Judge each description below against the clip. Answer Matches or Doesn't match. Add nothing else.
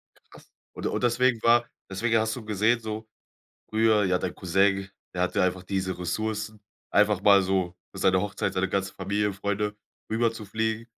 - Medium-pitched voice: Doesn't match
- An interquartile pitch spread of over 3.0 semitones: Doesn't match